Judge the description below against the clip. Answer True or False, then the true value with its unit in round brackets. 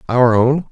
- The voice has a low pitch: True (125 Hz)